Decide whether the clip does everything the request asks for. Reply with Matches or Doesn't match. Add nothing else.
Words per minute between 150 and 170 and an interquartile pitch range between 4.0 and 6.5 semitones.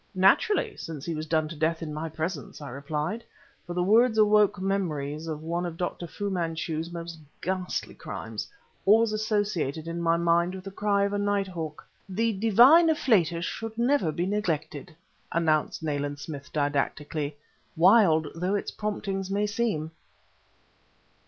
Matches